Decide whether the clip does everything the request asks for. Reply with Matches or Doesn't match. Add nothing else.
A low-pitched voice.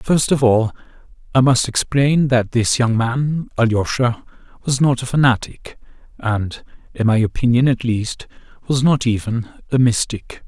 Matches